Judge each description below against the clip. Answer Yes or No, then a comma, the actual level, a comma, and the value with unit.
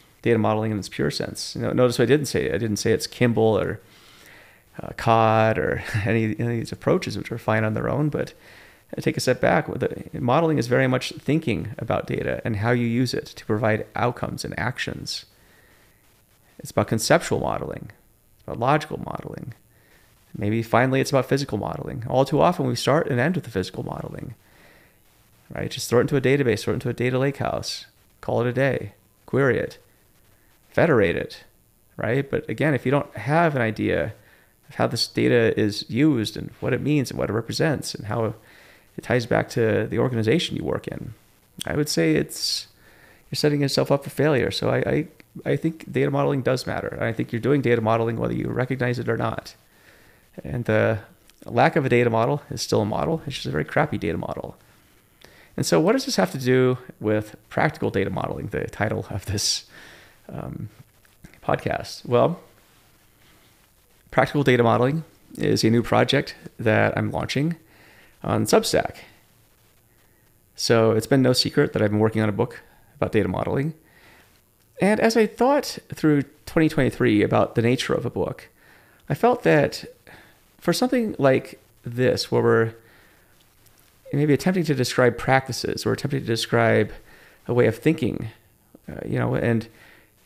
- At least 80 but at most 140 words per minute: No, average, 180 wpm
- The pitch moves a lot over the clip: No, average, 4.6 semitones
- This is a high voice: No, low, 120 Hz